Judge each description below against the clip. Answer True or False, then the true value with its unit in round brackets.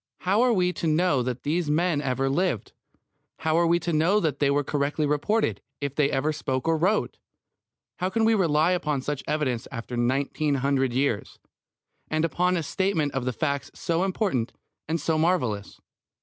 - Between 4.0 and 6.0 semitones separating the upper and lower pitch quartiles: True (4.4 semitones)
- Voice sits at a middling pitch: True (150 Hz)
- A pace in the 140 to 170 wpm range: False (180 wpm)